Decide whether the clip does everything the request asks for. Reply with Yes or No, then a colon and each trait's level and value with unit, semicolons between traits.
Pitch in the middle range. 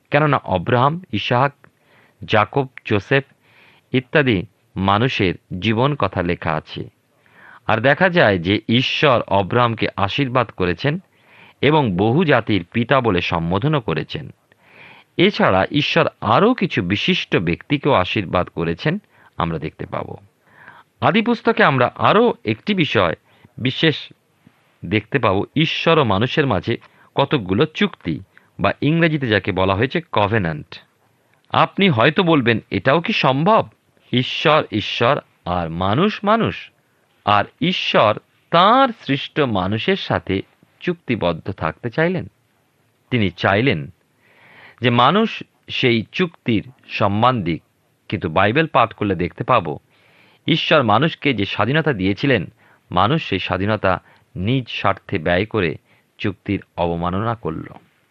No: low, 120 Hz